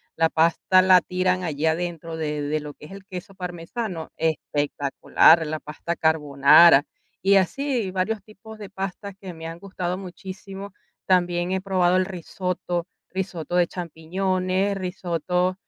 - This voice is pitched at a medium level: Yes, medium, 180 Hz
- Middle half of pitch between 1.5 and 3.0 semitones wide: Yes, narrow, 2.6 semitones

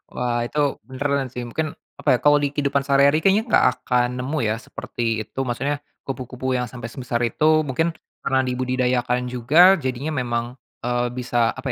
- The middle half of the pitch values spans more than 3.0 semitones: No, narrow, 2.5 semitones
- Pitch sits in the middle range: No, low, 130 Hz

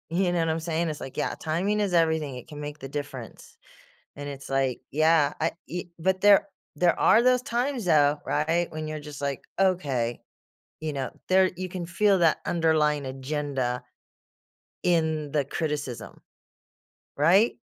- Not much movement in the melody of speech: No, average, 3.7 semitones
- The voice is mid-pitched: Yes, medium, 155 Hz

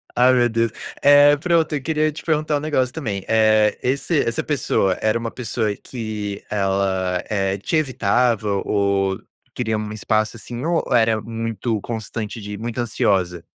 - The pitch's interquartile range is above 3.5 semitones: Yes, average, 3.9 semitones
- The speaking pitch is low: Yes, low, 115 Hz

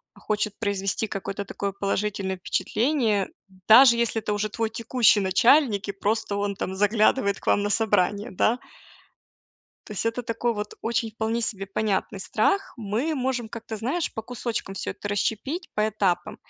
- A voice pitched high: Yes, high, 215 Hz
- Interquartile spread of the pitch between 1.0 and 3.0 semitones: Yes, narrow, 2.6 semitones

